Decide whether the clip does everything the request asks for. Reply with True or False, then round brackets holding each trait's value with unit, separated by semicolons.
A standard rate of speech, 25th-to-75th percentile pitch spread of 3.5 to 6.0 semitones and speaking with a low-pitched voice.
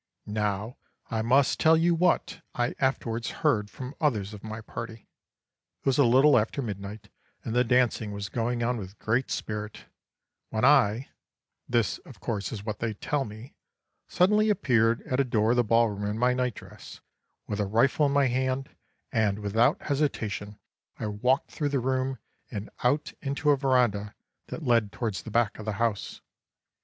True (175 wpm; 3.8 semitones; 115 Hz)